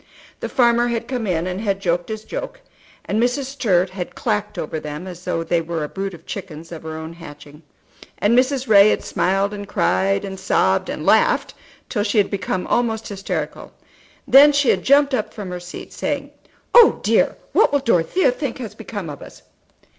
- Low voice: No, high, 200 Hz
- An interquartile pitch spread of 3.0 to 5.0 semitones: No, wide, 5.4 semitones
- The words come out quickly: No, average, 195 wpm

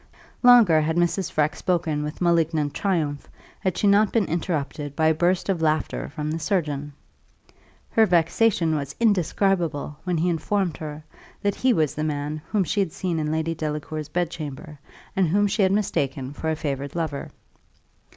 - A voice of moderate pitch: Yes, medium, 160 Hz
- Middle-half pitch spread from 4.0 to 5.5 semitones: No, average, 3.6 semitones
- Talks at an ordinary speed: Yes, average, 170 wpm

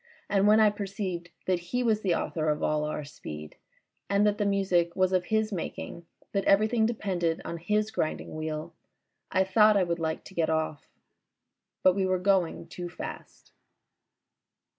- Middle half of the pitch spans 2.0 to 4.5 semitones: Yes, average, 3.5 semitones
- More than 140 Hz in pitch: Yes, medium, 185 Hz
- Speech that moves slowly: No, average, 170 wpm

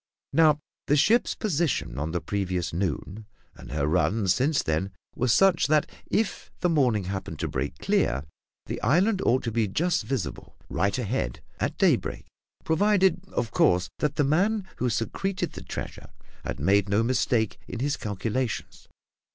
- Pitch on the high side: No, low, 120 Hz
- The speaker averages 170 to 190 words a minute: No, average, 160 wpm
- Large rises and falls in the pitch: Yes, wide, 8.4 semitones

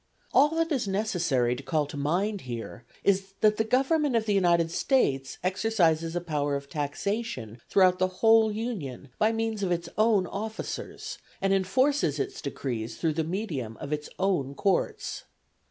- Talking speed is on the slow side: No, average, 165 wpm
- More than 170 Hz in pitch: Yes, medium, 185 Hz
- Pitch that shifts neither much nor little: No, wide, 7.1 semitones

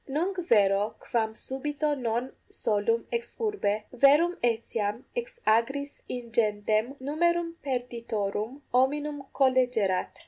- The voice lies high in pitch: Yes, high, 245 Hz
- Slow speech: Yes, slow, 100 wpm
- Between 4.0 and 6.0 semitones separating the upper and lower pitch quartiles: Yes, average, 4.8 semitones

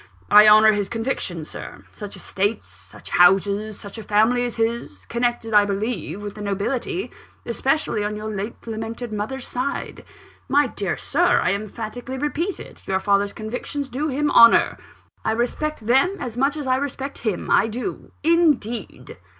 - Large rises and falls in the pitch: No, average, 4.3 semitones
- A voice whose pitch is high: Yes, high, 225 Hz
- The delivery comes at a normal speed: Yes, average, 160 wpm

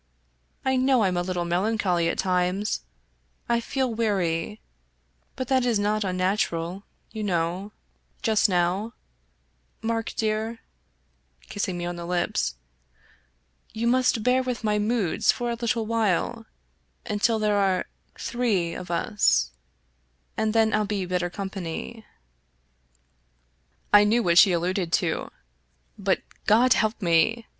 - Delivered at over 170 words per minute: No, slow, 135 wpm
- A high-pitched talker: Yes, high, 205 Hz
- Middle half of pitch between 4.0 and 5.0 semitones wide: Yes, average, 4.3 semitones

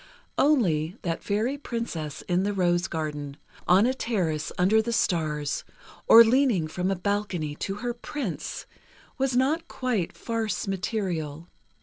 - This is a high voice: Yes, high, 195 Hz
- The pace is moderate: No, slow, 130 wpm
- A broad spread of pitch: Yes, wide, 5.9 semitones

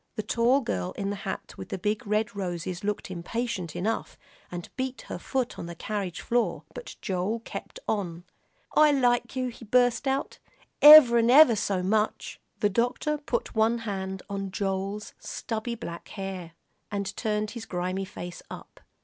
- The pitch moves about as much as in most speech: Yes, average, 3.9 semitones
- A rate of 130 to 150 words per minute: No, average, 160 wpm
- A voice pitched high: Yes, high, 210 Hz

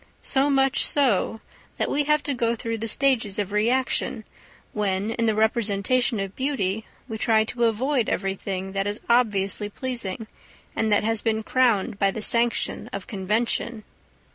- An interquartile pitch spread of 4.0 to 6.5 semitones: No, average, 3.3 semitones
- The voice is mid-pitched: No, high, 220 Hz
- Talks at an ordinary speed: Yes, average, 160 wpm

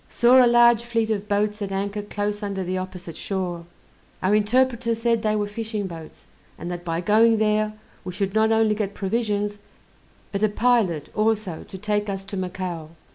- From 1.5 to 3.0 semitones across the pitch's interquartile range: Yes, average, 2.7 semitones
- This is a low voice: No, high, 210 Hz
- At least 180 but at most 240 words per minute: Yes, average, 185 wpm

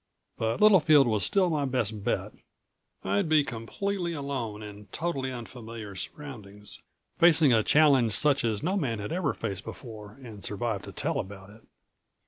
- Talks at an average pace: Yes, average, 155 wpm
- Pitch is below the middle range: Yes, low, 120 Hz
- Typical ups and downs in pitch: No, wide, 6.0 semitones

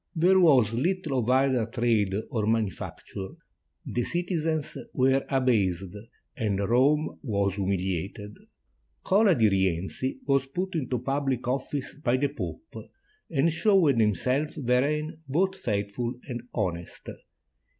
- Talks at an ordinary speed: No, slow, 120 wpm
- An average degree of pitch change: No, wide, 6.2 semitones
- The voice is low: Yes, low, 130 Hz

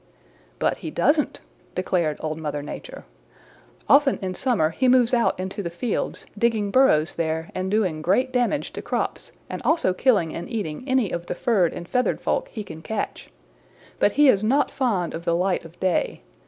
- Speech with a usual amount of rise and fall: No, wide, 6.6 semitones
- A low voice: No, high, 195 Hz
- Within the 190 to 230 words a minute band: No, average, 180 wpm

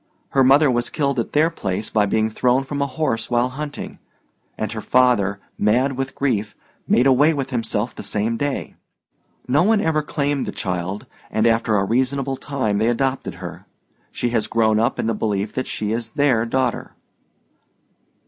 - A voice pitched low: Yes, low, 120 Hz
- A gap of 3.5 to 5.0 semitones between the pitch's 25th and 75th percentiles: Yes, average, 4.0 semitones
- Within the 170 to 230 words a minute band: Yes, average, 175 wpm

